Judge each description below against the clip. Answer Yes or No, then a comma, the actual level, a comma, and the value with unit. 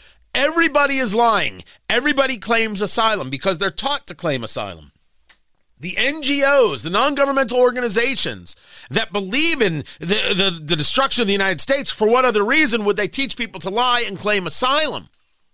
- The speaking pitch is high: Yes, high, 220 Hz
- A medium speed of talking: Yes, average, 160 wpm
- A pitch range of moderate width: No, wide, 6.2 semitones